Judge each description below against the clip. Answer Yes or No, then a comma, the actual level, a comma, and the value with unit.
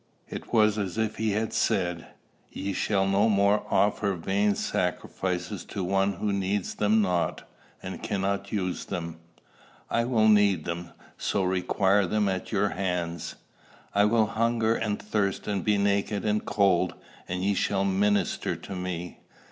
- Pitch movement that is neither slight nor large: No, narrow, 2.1 semitones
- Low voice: Yes, low, 100 Hz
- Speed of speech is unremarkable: Yes, average, 155 wpm